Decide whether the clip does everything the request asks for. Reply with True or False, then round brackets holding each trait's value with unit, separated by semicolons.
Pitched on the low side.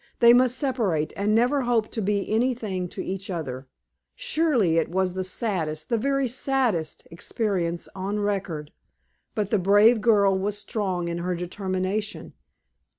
False (200 Hz)